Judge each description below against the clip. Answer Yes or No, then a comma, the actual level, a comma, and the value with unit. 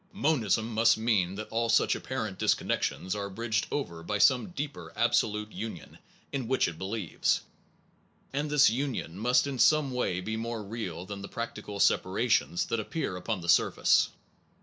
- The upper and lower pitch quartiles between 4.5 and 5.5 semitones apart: No, average, 4.1 semitones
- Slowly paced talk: No, average, 160 wpm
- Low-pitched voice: Yes, low, 110 Hz